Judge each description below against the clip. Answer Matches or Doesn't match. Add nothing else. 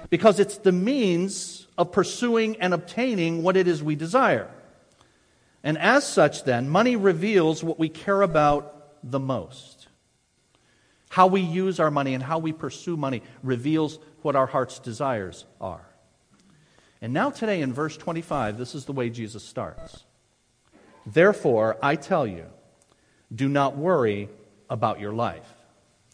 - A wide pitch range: Matches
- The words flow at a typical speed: Matches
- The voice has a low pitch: Doesn't match